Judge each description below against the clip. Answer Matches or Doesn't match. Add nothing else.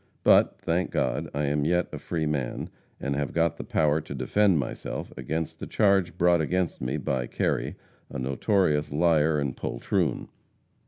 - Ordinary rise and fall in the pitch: Matches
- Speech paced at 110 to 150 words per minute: Doesn't match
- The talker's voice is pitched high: Doesn't match